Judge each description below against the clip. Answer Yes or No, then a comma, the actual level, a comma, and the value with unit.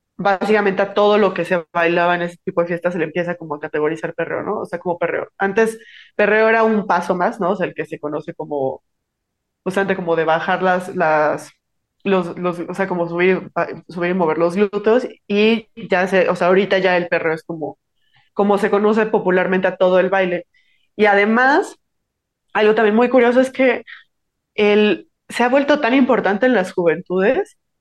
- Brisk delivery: Yes, fast, 195 wpm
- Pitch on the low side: No, medium, 185 Hz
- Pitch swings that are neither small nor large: Yes, average, 3.4 semitones